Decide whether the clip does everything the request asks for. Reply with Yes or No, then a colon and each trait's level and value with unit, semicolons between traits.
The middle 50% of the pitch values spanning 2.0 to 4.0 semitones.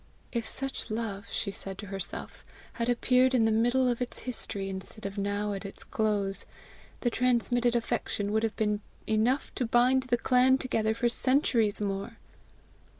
Yes: average, 3.3 semitones